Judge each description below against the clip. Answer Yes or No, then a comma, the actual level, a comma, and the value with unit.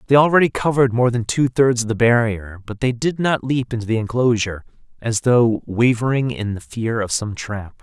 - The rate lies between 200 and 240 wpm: Yes, fast, 205 wpm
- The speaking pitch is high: No, low, 120 Hz